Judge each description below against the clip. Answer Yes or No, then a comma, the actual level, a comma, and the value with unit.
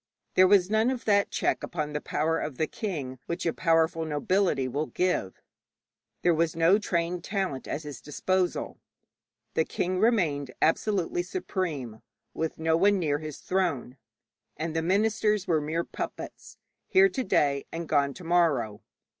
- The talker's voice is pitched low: No, medium, 165 Hz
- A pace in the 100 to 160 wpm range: Yes, average, 155 wpm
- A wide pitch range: No, average, 4.0 semitones